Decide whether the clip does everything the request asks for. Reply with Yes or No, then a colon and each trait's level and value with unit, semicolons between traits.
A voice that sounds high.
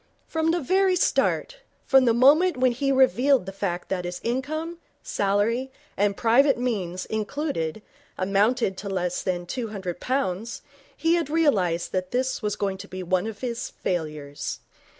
Yes: high, 225 Hz